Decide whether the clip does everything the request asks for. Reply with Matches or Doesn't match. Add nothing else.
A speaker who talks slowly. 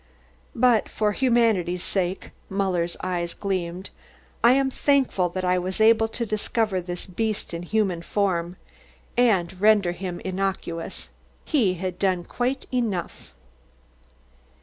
Matches